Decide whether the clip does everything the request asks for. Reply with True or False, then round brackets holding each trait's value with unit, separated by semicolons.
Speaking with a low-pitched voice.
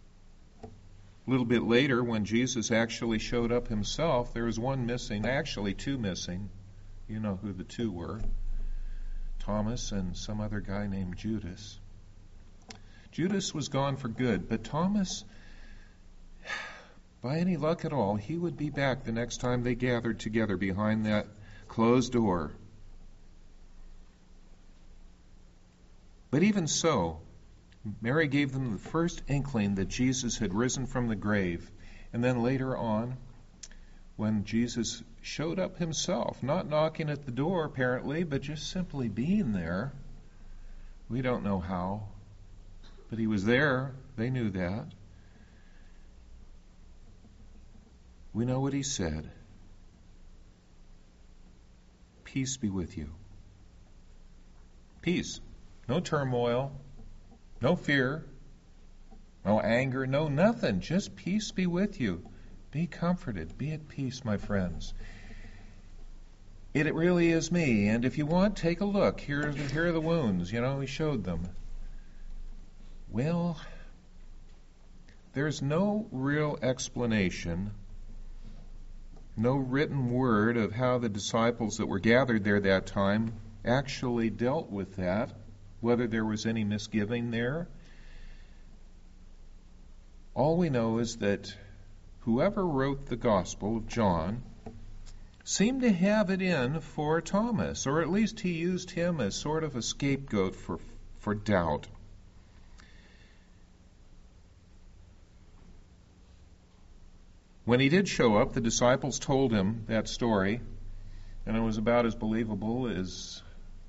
True (110 Hz)